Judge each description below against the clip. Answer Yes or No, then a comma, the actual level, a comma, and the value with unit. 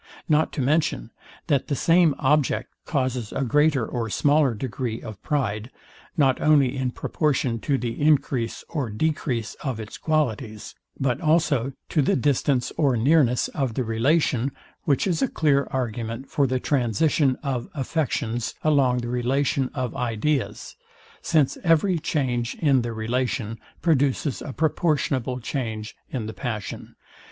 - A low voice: Yes, low, 130 Hz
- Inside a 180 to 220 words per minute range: No, average, 145 wpm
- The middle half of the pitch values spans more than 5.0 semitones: No, average, 3.8 semitones